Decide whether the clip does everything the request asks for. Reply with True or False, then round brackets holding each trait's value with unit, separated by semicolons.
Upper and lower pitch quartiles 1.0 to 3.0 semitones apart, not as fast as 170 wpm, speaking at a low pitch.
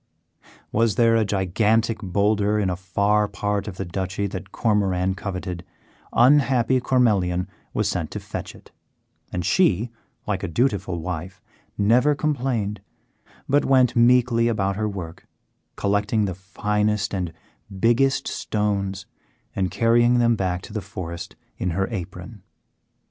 False (3.5 semitones; 135 wpm; 105 Hz)